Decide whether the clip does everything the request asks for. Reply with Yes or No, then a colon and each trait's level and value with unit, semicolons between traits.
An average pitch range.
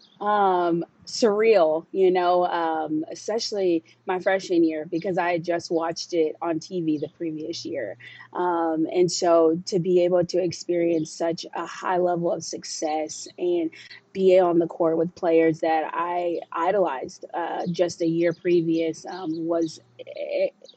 No: narrow, 2.1 semitones